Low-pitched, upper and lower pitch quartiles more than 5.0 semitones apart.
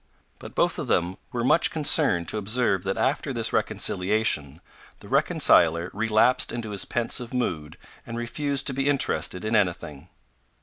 Yes: low, 110 Hz; wide, 5.6 semitones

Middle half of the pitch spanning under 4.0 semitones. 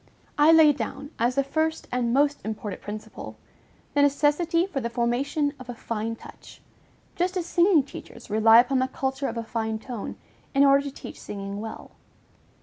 No: average, 4.3 semitones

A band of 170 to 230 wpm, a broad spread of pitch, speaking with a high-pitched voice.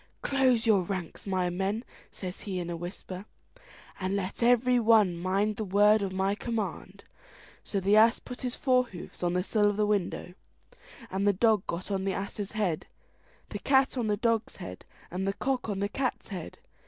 No: average, 185 wpm; average, 3.3 semitones; high, 200 Hz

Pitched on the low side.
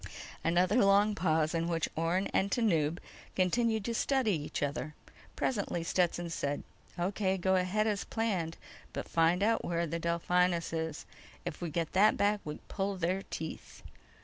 No: medium, 180 Hz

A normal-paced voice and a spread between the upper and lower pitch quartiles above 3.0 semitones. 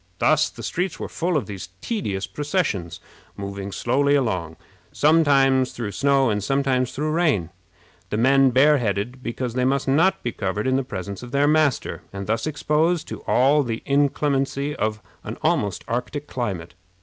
Yes: average, 160 wpm; wide, 5.5 semitones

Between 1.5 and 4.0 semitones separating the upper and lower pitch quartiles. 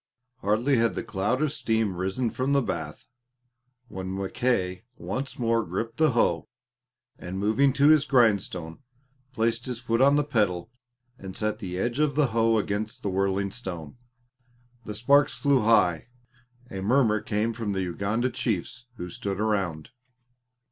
No: average, 4.6 semitones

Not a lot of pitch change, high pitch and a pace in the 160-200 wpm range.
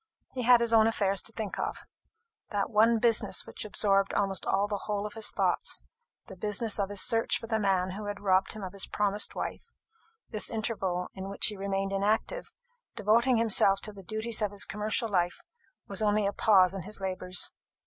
Yes: narrow, 2.0 semitones; high, 205 Hz; average, 195 wpm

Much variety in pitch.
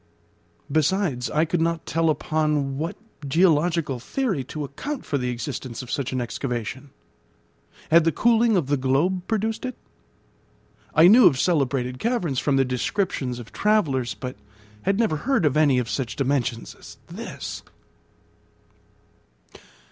Yes: wide, 5.7 semitones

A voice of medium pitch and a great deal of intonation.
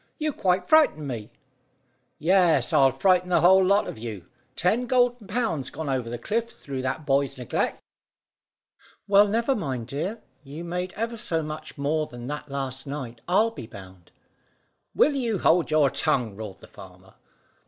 Yes: medium, 155 Hz; wide, 7.3 semitones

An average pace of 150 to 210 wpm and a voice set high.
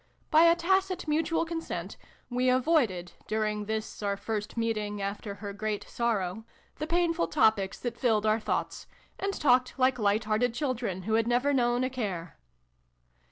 Yes: average, 160 wpm; high, 230 Hz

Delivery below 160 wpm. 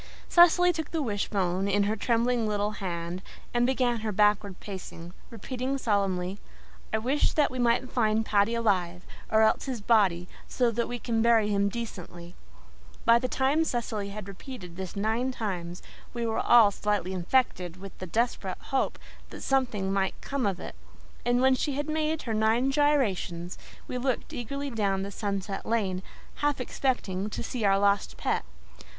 No: average, 170 wpm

